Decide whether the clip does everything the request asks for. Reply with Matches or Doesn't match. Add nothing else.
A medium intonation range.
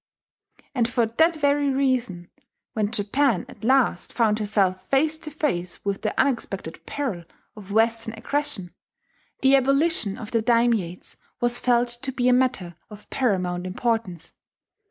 Matches